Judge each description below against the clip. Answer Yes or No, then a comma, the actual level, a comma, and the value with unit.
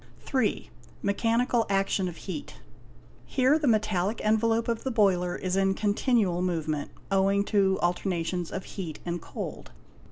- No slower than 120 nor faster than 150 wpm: Yes, slow, 135 wpm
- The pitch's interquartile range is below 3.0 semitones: No, average, 3.9 semitones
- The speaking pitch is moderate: No, high, 195 Hz